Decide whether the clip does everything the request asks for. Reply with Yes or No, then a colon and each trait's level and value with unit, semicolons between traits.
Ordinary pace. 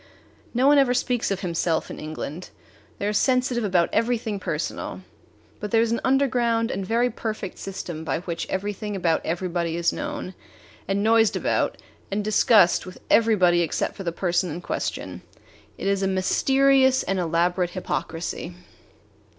Yes: average, 150 wpm